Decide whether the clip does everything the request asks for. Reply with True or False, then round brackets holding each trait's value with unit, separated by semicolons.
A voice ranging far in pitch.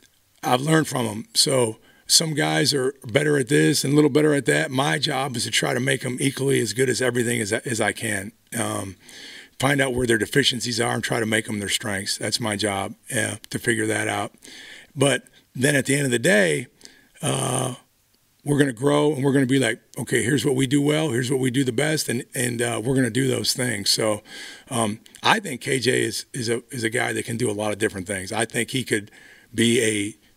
False (3.7 semitones)